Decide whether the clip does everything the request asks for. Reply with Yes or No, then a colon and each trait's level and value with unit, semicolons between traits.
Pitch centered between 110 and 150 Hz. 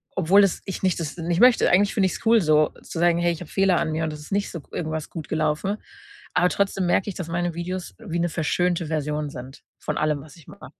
No: medium, 170 Hz